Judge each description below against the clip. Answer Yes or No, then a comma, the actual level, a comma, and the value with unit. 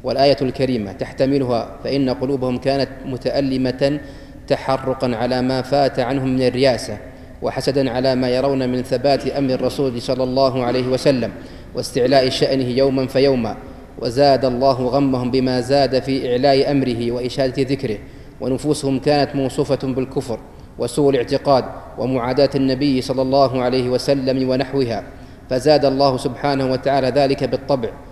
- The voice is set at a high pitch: No, low, 130 Hz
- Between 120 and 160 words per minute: Yes, average, 125 wpm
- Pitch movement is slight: Yes, narrow, 1.3 semitones